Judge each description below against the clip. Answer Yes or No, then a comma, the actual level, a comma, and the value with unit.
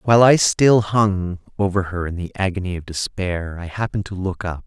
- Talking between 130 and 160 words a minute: No, fast, 205 wpm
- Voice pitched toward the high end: No, very low, 95 Hz